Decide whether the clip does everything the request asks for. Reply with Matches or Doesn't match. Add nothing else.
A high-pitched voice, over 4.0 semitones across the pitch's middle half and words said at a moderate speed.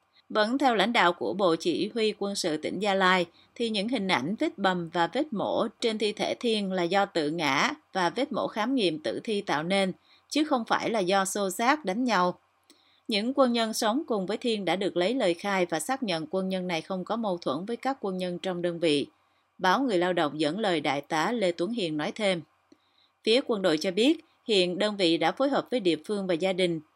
Matches